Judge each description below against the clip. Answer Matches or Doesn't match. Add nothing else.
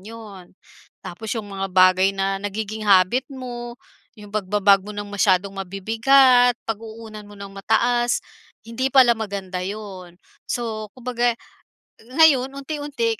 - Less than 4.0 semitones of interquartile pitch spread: Matches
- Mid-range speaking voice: Doesn't match